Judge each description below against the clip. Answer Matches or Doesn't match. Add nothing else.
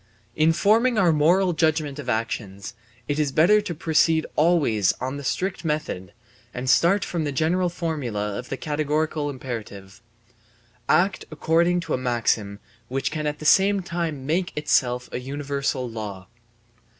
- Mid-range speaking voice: Matches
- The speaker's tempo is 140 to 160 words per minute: Matches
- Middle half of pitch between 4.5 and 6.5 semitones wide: Matches